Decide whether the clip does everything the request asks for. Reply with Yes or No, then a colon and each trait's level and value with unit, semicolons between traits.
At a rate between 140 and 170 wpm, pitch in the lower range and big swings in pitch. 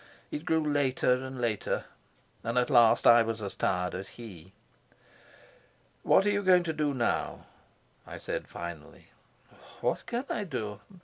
Yes: average, 150 wpm; low, 125 Hz; wide, 6.5 semitones